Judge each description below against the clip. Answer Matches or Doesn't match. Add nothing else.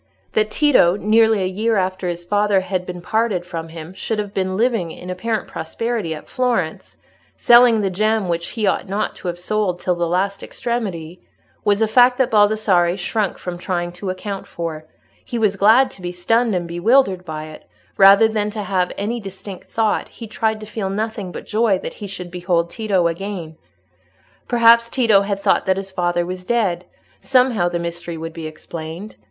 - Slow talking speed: Doesn't match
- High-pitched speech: Matches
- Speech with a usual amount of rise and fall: Matches